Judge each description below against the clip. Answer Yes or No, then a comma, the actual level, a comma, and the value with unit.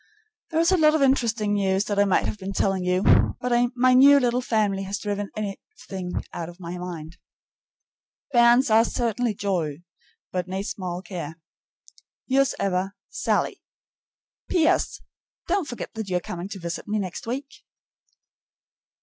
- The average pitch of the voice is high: Yes, high, 205 Hz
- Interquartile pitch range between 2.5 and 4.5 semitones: No, average, 4.9 semitones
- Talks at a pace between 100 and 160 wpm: Yes, average, 155 wpm